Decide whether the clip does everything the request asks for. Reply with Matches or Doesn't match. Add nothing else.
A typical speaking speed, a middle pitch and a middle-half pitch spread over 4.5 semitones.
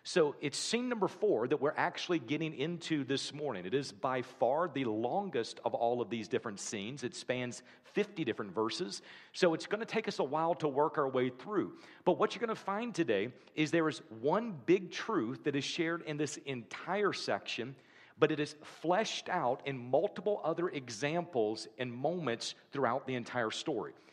Matches